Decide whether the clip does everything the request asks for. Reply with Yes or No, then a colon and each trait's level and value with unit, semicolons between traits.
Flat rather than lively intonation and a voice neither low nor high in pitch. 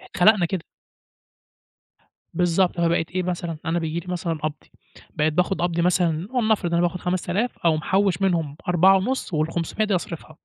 Yes: narrow, 2.3 semitones; medium, 175 Hz